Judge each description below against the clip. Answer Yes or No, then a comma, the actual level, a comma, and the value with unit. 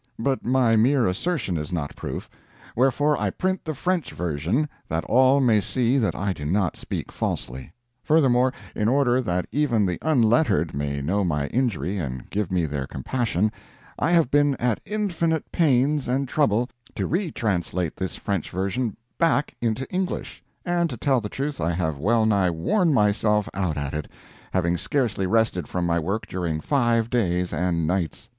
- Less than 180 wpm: Yes, average, 170 wpm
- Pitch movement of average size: No, wide, 7.5 semitones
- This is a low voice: Yes, low, 110 Hz